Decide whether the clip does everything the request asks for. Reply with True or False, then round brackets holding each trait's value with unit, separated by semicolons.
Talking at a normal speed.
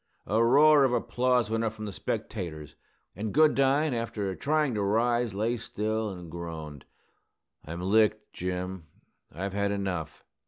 True (145 wpm)